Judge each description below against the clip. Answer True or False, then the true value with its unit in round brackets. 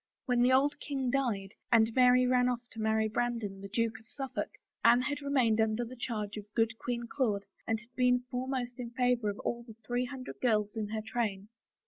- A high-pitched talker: True (240 Hz)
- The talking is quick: True (210 wpm)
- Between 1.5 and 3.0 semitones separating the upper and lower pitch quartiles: True (2.4 semitones)